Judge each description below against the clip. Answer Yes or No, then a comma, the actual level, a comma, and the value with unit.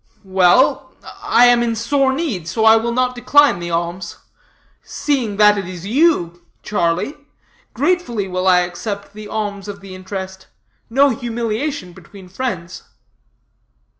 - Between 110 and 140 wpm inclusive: Yes, slow, 135 wpm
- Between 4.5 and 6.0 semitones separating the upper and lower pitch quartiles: Yes, average, 4.8 semitones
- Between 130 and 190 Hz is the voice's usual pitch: No, high, 210 Hz